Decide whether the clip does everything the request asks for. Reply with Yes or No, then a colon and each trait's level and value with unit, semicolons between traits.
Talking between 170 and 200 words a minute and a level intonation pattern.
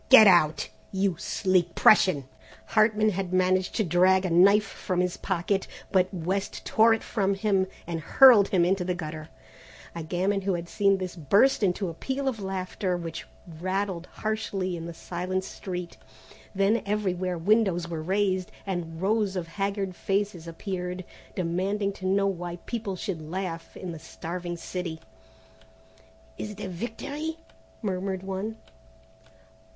No: average, 150 wpm; narrow, 2.3 semitones